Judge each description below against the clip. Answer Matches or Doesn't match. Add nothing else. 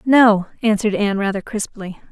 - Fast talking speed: Doesn't match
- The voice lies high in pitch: Matches